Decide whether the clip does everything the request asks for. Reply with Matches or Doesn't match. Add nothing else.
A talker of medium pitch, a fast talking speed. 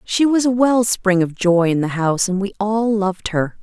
Doesn't match